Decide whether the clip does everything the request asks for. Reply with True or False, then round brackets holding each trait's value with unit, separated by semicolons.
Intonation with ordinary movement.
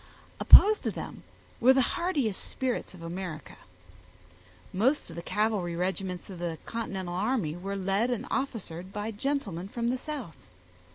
False (5.8 semitones)